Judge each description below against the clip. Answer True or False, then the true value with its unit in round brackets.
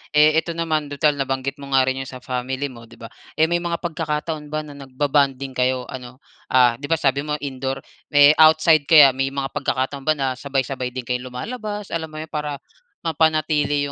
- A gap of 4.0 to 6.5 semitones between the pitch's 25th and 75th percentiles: False (2.9 semitones)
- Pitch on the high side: False (140 Hz)